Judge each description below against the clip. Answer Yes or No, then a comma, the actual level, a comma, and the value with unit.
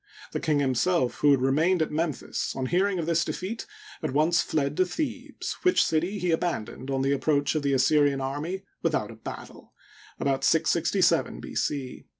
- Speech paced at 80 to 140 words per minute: No, average, 175 wpm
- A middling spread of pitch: Yes, average, 3.9 semitones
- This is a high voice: No, medium, 155 Hz